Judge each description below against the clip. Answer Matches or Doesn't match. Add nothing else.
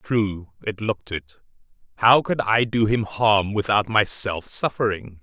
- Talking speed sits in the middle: Matches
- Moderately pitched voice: Doesn't match